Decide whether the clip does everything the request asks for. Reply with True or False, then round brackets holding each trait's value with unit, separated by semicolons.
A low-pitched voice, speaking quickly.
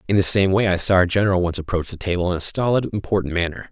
True (95 Hz; 275 wpm)